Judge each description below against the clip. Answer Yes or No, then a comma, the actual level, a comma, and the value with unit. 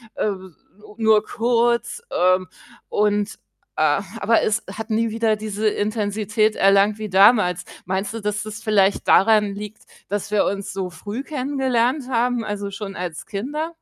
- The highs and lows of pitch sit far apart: No, narrow, 2.4 semitones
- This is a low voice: No, high, 210 Hz